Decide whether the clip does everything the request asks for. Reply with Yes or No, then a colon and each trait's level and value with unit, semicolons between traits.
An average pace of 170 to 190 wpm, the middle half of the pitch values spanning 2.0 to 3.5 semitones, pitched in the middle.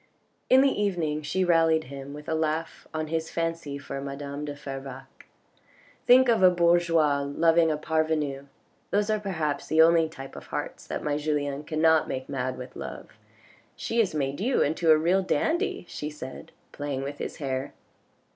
Yes: average, 175 wpm; average, 3.0 semitones; medium, 155 Hz